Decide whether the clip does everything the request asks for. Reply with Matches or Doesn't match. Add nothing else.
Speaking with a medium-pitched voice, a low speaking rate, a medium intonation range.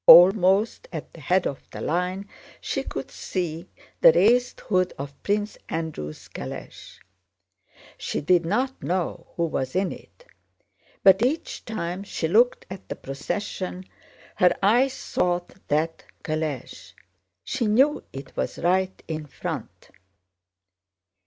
Matches